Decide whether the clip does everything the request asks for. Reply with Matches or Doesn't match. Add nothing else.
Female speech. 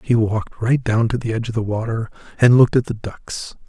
Doesn't match